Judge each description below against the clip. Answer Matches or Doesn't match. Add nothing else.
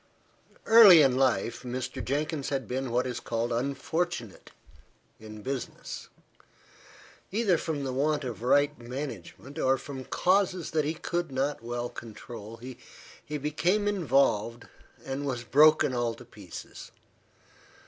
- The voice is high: Doesn't match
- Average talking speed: Doesn't match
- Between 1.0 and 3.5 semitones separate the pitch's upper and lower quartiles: Doesn't match